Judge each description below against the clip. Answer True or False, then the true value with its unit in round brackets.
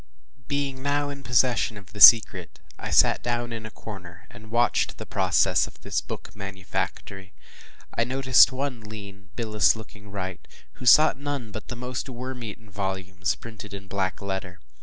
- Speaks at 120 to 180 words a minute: True (165 wpm)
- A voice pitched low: True (110 Hz)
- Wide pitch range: False (4.3 semitones)